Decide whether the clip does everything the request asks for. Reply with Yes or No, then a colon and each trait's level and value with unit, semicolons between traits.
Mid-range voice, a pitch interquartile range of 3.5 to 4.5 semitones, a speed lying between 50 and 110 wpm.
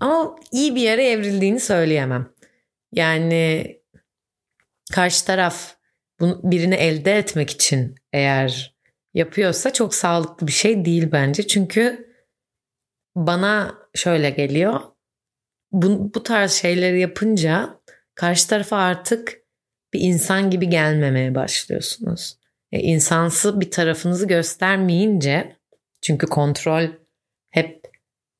Yes: medium, 175 Hz; average, 4.0 semitones; average, 100 wpm